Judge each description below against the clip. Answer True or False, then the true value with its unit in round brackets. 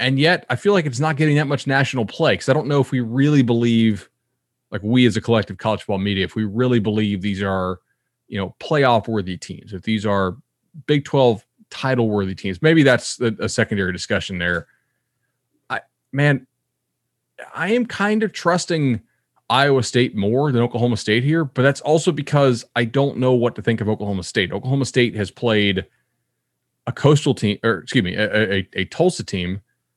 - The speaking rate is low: False (190 wpm)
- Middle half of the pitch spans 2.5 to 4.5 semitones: False (5.3 semitones)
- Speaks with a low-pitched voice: True (120 Hz)